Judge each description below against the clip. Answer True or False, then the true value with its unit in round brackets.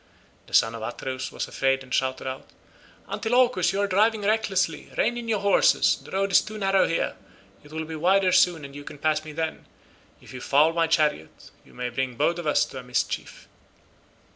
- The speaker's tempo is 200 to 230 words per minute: True (205 wpm)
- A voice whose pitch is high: False (160 Hz)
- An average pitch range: False (6.6 semitones)